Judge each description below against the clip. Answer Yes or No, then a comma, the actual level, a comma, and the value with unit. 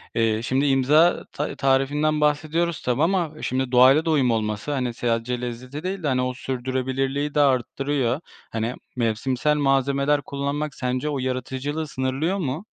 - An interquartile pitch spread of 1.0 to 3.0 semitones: Yes, average, 2.7 semitones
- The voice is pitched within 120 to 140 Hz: Yes, low, 135 Hz